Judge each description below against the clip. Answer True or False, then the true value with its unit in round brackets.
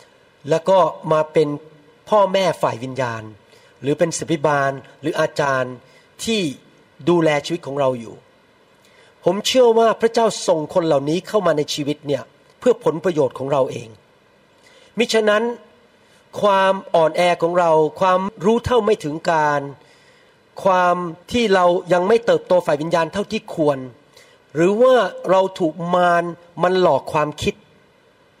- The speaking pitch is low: False (175 Hz)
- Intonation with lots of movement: True (5.9 semitones)